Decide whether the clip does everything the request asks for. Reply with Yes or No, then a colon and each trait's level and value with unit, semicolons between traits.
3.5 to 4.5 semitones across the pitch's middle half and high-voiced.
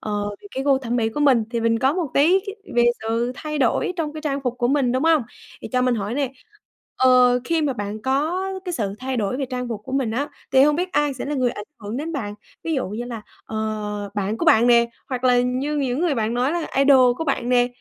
Yes: average, 3.8 semitones; very high, 255 Hz